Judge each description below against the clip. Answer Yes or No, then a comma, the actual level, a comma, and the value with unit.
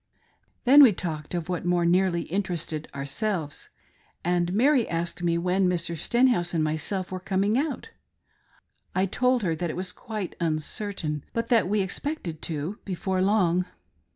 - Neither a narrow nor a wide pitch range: Yes, average, 3.6 semitones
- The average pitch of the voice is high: No, medium, 180 Hz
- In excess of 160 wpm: No, average, 155 wpm